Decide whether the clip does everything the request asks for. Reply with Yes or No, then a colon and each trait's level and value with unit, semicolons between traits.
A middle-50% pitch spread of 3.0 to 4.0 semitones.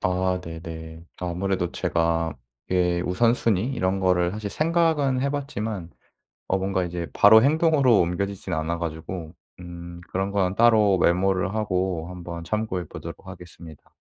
Yes: average, 3.7 semitones